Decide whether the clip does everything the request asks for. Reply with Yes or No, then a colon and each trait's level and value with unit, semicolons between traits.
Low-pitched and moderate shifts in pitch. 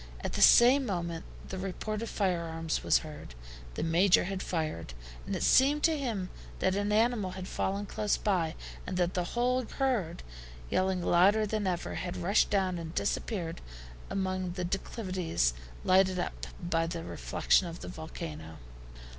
No: medium, 185 Hz; average, 3.4 semitones